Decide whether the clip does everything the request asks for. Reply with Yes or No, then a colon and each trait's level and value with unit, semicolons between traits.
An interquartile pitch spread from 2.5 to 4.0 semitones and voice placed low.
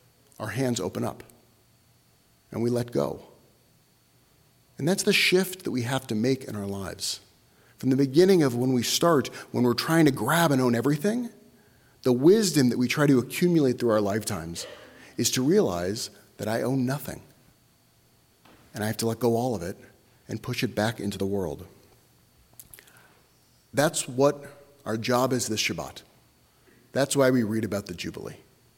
No: average, 4.4 semitones; low, 125 Hz